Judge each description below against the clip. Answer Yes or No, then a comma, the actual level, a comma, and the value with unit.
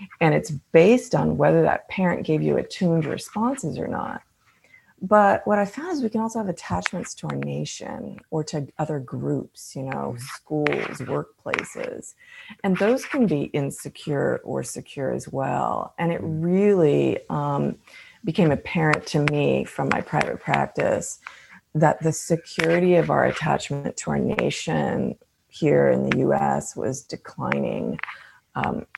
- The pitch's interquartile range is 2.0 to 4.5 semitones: No, wide, 5.6 semitones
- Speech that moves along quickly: No, average, 145 wpm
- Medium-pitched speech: Yes, medium, 165 Hz